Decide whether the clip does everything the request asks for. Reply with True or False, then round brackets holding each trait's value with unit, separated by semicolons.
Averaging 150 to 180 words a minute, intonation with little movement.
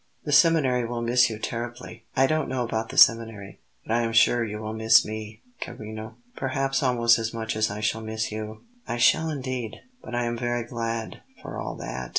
False (200 wpm; 2.1 semitones)